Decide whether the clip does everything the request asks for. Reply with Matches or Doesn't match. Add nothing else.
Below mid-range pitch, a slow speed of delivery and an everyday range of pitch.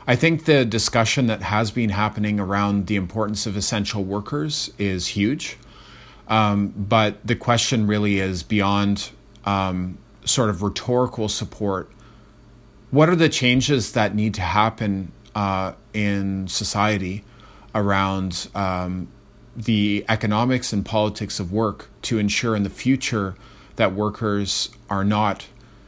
Doesn't match